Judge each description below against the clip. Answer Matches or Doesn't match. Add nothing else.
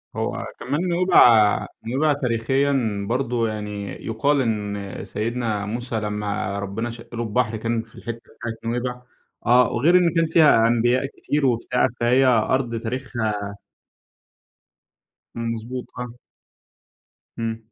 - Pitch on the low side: Matches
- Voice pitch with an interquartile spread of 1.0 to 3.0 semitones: Matches